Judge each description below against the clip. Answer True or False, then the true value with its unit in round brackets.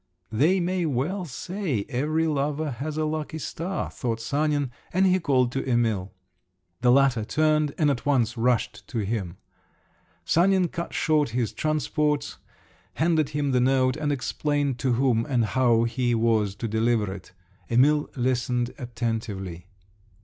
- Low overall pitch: True (130 Hz)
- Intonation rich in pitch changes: False (4.6 semitones)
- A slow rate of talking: False (145 wpm)